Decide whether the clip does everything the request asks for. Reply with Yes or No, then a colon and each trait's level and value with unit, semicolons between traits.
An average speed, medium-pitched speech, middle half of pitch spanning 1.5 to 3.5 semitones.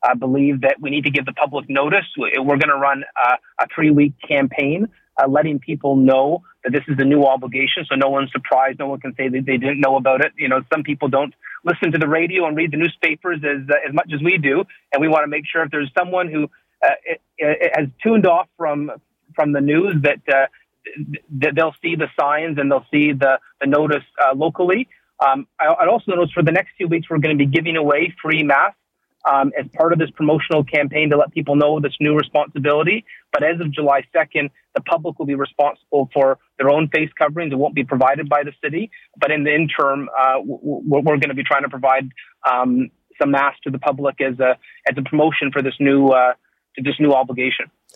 No: fast, 230 wpm; medium, 145 Hz; narrow, 2.5 semitones